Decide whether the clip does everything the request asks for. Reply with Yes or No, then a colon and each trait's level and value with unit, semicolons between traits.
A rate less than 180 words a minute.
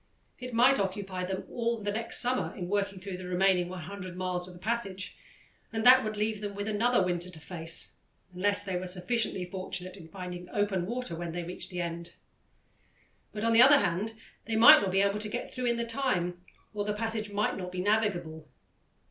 No: fast, 205 wpm